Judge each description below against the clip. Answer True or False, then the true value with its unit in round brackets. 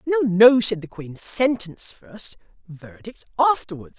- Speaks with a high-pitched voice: True (210 Hz)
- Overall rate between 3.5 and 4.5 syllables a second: True (4.1 syllables/s)